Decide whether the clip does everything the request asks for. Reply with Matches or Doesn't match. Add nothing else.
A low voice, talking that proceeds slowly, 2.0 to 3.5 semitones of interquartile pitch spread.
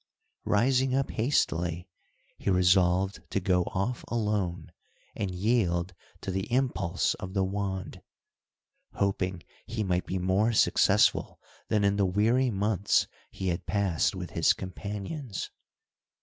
Matches